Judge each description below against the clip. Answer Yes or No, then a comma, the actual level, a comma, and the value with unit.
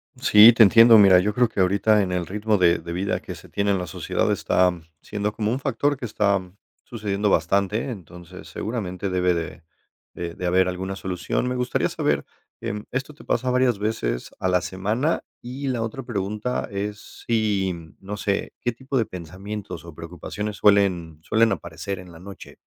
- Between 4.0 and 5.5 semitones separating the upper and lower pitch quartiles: No, average, 3.6 semitones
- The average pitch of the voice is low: Yes, low, 100 Hz